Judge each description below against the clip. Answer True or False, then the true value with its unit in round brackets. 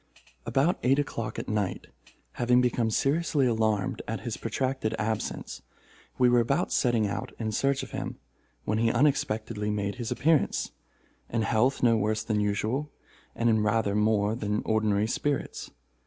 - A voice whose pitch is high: False (115 Hz)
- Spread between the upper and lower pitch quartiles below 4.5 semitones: True (3.1 semitones)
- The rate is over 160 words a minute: False (155 wpm)